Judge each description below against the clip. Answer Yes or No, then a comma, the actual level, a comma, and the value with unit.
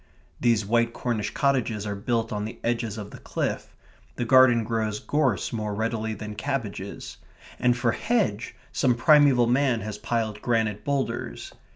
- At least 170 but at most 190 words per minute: No, average, 155 wpm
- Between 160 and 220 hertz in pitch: No, low, 115 Hz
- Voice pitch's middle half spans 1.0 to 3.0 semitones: Yes, average, 2.7 semitones